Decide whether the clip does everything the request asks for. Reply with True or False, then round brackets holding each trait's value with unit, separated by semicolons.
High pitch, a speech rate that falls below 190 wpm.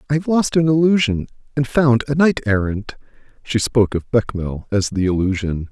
False (120 Hz; 180 wpm)